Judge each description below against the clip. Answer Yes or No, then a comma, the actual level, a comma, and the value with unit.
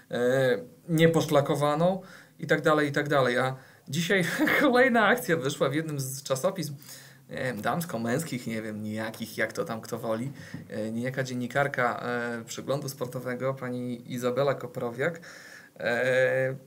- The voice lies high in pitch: No, low, 135 Hz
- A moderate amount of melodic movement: Yes, average, 4.1 semitones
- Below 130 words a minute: No, average, 135 wpm